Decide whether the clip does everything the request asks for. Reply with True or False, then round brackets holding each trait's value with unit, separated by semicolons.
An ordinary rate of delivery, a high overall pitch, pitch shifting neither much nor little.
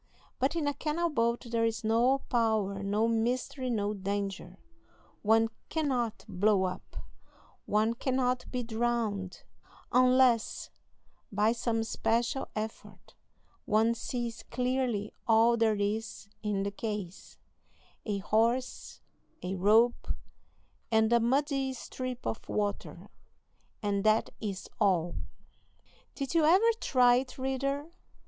False (115 wpm; 230 Hz; 3.4 semitones)